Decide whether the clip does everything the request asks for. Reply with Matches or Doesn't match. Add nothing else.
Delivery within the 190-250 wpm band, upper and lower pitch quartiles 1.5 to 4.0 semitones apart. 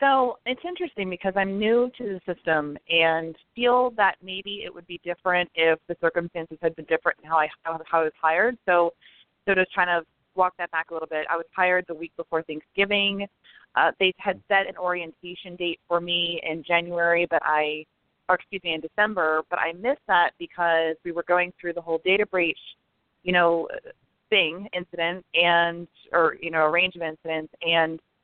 Matches